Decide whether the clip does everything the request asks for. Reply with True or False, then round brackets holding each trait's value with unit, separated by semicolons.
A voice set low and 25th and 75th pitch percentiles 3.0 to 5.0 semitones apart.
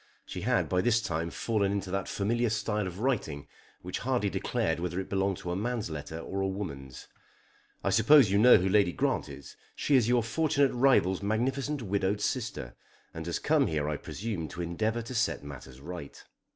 False (100 Hz; 5.4 semitones)